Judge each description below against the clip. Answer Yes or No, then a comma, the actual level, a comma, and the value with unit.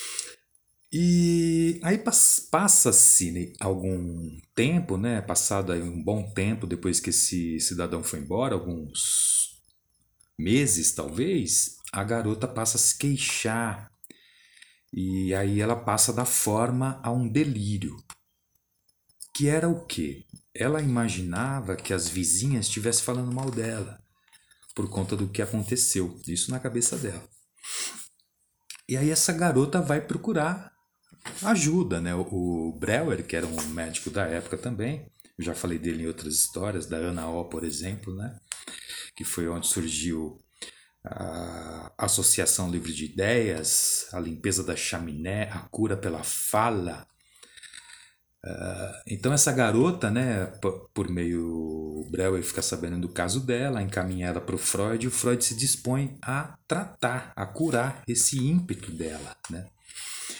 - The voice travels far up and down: Yes, wide, 6.1 semitones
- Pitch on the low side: Yes, low, 100 Hz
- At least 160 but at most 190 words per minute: No, average, 135 wpm